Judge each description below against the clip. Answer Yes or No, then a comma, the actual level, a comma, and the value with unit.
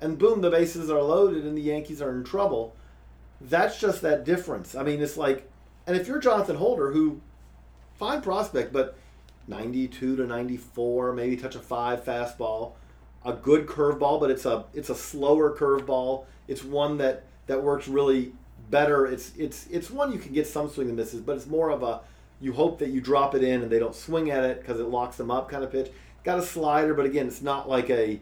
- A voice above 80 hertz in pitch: Yes, low, 135 Hz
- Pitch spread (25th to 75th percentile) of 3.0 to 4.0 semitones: Yes, average, 3.6 semitones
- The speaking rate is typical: No, fast, 215 wpm